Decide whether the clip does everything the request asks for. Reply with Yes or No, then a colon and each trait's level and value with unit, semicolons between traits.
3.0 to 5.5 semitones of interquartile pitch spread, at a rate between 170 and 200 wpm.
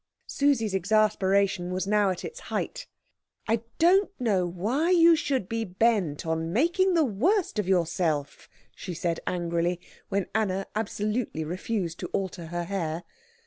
No: average, 4.9 semitones; average, 145 wpm